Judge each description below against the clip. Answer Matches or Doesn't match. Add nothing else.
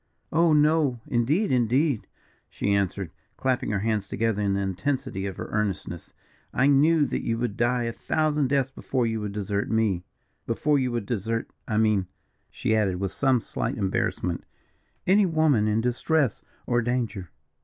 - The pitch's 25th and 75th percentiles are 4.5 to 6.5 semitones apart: Matches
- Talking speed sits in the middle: Matches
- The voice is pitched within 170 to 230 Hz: Doesn't match